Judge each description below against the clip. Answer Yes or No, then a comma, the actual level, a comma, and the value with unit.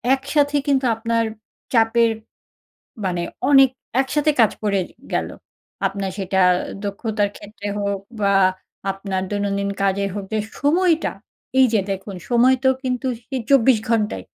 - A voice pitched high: Yes, high, 220 Hz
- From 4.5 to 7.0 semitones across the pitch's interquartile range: Yes, average, 4.9 semitones